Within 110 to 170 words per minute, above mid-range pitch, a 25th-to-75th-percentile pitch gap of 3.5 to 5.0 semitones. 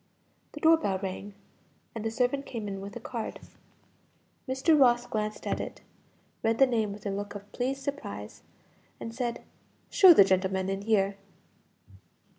Yes: average, 160 wpm; high, 220 Hz; average, 4.1 semitones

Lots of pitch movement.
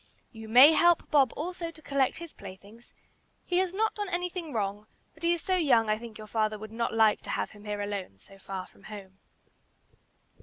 Yes: wide, 8.3 semitones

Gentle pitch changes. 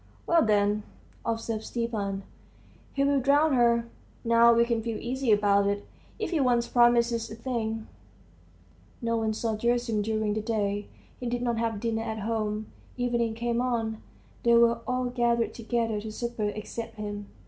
Yes: narrow, 1.9 semitones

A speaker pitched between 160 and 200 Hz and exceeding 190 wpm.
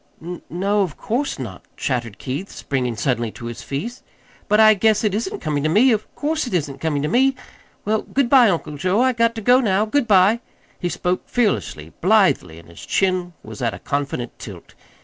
Yes: high, 190 Hz; average, 200 wpm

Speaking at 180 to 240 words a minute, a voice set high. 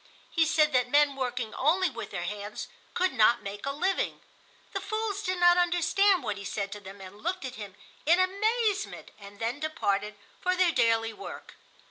Yes: average, 185 wpm; very high, 285 Hz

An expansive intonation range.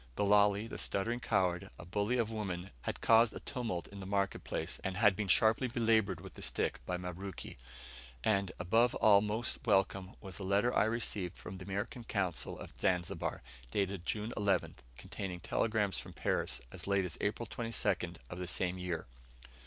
No: average, 3.1 semitones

